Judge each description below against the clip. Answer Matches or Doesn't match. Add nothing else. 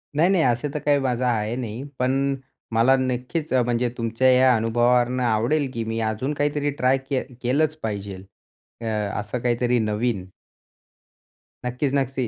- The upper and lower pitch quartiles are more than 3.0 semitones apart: Doesn't match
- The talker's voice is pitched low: Matches